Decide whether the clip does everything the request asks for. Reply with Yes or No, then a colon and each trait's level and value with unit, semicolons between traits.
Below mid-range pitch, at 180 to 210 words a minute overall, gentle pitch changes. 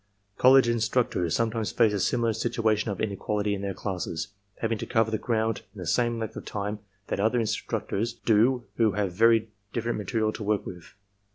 Yes: low, 110 Hz; average, 185 wpm; narrow, 2.2 semitones